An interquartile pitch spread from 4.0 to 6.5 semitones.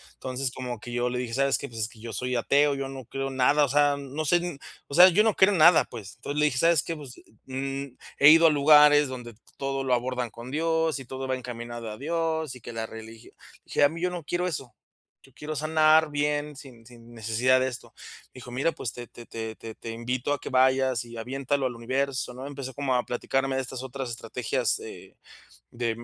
No: average, 3.2 semitones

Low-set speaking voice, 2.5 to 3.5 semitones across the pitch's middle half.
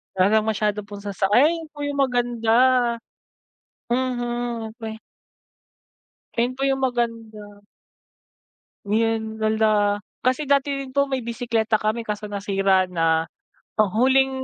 No: high, 225 Hz; average, 3.2 semitones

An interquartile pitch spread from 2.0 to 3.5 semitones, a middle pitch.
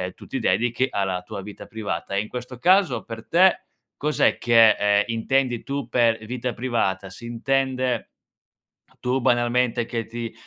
No: narrow, 2.4 semitones; low, 120 Hz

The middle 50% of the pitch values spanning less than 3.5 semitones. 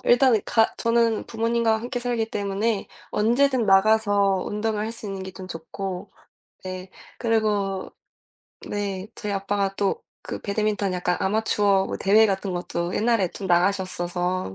Yes: average, 2.7 semitones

